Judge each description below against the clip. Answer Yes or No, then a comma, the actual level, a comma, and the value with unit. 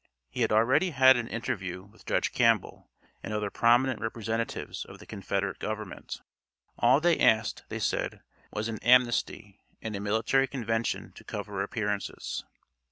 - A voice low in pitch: Yes, low, 110 Hz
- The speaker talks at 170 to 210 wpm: No, average, 150 wpm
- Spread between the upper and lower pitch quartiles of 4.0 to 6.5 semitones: No, average, 2.8 semitones